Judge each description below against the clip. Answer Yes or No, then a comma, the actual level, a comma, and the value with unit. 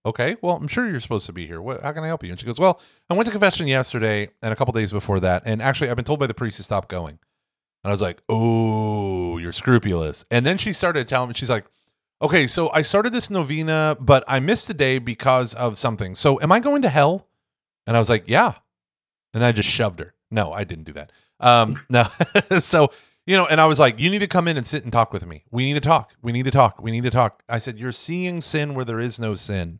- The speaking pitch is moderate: No, low, 125 Hz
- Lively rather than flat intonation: Yes, wide, 6.5 semitones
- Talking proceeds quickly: Yes, fast, 270 wpm